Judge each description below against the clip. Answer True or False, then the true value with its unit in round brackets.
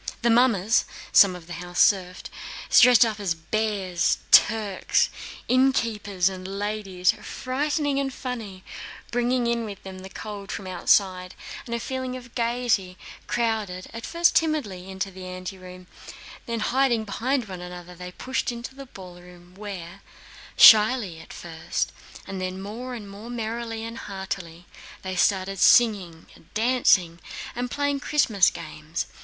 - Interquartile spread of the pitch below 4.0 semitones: False (4.6 semitones)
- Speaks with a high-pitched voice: True (205 Hz)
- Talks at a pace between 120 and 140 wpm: True (135 wpm)